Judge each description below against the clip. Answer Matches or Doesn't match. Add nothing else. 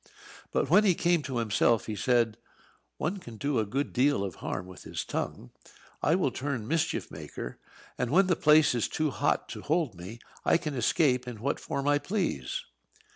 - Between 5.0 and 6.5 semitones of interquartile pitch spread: Matches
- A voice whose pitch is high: Doesn't match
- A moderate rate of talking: Matches